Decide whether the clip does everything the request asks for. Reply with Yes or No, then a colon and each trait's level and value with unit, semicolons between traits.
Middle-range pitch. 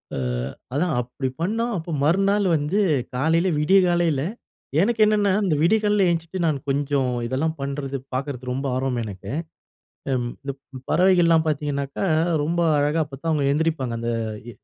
Yes: medium, 155 Hz